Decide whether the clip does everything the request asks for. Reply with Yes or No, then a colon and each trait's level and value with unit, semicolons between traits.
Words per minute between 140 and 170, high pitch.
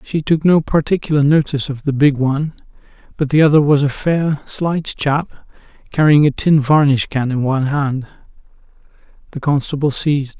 No: average, 160 wpm; medium, 145 Hz